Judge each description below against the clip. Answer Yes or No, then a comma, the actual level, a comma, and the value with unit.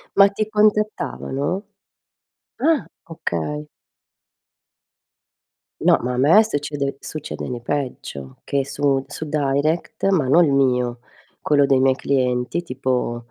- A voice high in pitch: No, medium, 140 Hz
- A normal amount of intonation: Yes, average, 4.0 semitones